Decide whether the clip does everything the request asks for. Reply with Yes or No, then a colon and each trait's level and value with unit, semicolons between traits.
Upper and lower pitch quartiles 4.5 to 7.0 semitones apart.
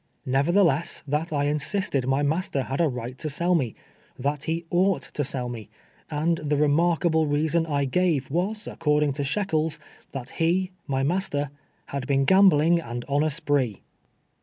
No: average, 3.6 semitones